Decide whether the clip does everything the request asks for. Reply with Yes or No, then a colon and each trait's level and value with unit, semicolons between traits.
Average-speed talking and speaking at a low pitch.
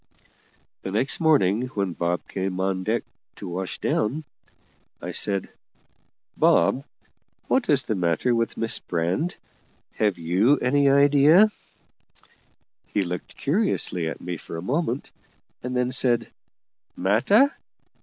No: slow, 125 wpm; low, 115 Hz